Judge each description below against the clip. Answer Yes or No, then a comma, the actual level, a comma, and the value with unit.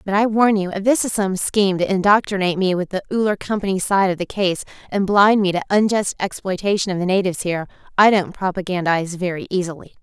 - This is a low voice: No, high, 190 Hz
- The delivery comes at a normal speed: No, fast, 210 wpm